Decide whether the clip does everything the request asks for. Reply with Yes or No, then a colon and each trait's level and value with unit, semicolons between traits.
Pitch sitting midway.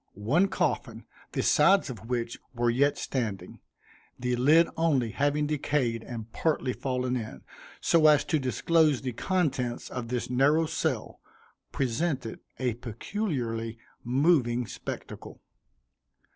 No: low, 130 Hz